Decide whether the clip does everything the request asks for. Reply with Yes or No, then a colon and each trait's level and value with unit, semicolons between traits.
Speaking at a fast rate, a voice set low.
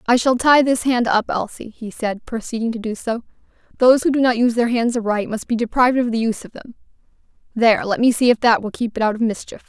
No: fast, 255 wpm; high, 235 Hz